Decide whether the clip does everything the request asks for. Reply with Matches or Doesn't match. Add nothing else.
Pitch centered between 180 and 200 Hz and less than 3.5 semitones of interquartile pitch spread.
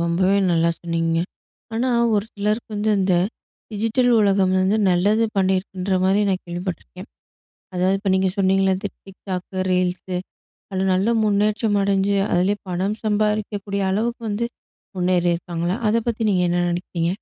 Matches